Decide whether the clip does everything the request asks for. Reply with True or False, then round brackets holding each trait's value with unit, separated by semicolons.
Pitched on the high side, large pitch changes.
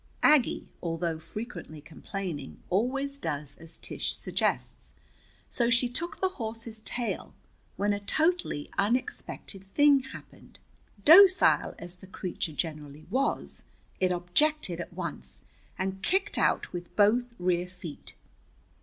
True (195 Hz; 6.9 semitones)